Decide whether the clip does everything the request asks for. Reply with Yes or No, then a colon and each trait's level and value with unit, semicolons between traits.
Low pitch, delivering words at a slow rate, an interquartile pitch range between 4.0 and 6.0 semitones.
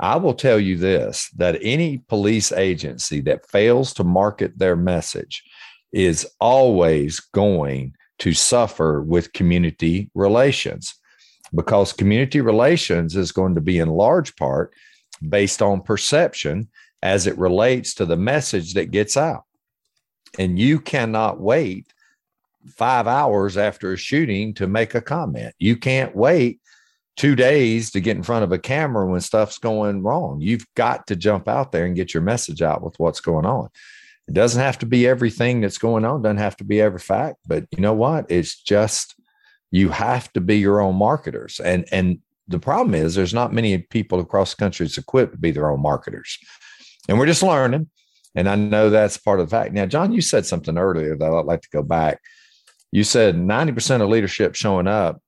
No: low, 105 Hz; average, 180 wpm; average, 4.6 semitones